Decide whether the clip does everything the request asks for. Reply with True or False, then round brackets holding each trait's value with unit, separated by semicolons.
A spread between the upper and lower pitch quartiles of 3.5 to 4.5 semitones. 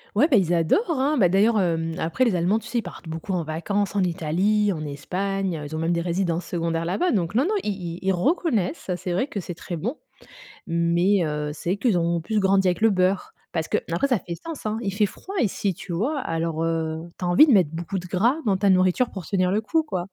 True (4.0 semitones)